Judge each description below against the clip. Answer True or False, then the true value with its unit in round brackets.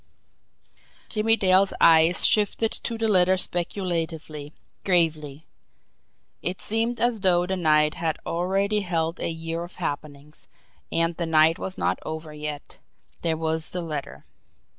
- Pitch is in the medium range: True (170 Hz)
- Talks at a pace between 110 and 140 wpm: True (135 wpm)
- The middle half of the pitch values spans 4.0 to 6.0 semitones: False (3.1 semitones)